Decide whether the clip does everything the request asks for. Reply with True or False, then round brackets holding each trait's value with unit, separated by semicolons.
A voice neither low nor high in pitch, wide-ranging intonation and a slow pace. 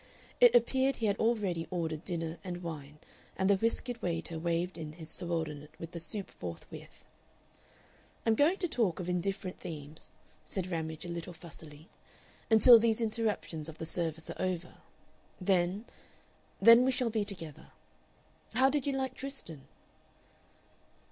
False (180 Hz; 5.7 semitones; 150 wpm)